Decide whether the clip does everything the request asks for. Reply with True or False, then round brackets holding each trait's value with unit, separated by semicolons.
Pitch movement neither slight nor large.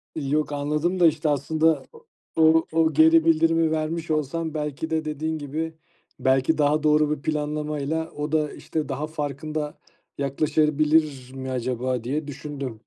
False (1.9 semitones)